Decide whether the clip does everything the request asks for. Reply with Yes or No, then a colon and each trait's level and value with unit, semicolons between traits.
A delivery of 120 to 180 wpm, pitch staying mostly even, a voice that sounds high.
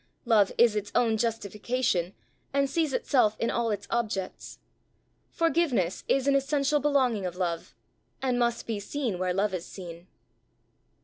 No: average, 145 wpm; wide, 5.5 semitones; high, 230 Hz